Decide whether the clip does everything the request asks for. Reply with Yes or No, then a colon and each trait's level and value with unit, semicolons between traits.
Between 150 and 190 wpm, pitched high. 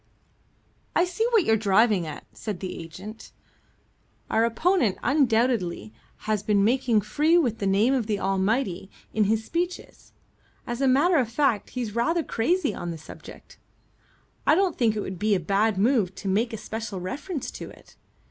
Yes: average, 170 wpm; high, 225 Hz